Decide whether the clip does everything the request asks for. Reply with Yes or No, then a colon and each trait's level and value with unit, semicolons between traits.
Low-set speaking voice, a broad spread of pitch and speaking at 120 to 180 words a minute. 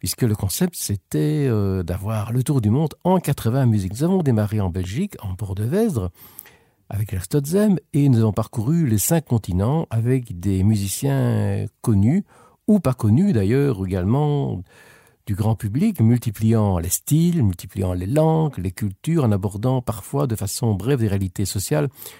Yes: low, 115 Hz; wide, 6.0 semitones; average, 160 wpm